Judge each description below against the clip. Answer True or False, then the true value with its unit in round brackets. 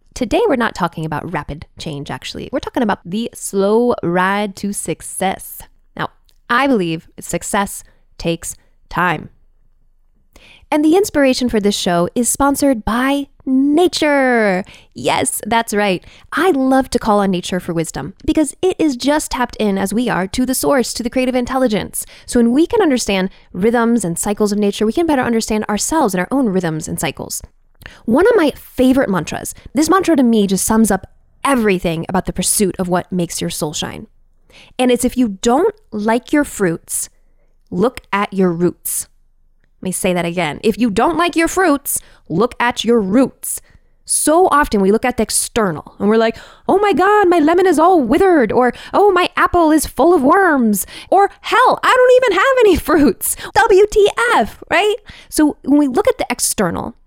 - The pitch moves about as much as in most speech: False (7.6 semitones)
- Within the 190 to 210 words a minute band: False (180 wpm)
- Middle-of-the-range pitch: False (235 Hz)